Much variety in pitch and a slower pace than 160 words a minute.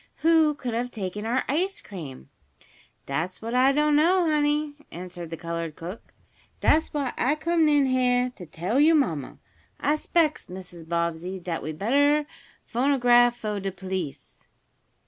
Yes: wide, 8.8 semitones; average, 150 wpm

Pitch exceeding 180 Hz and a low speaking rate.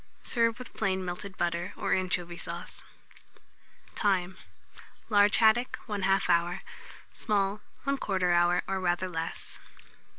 Yes: high, 190 Hz; slow, 110 wpm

